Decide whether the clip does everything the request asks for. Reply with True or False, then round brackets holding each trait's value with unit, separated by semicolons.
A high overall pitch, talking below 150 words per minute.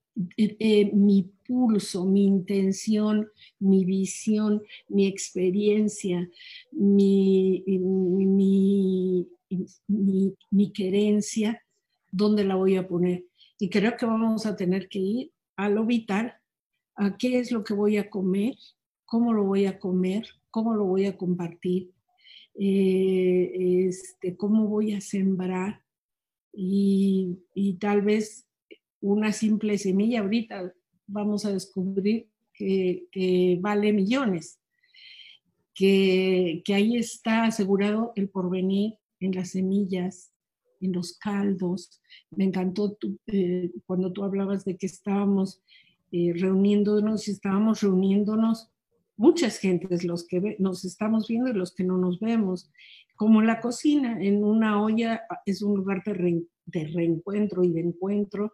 True (195 Hz; 130 wpm)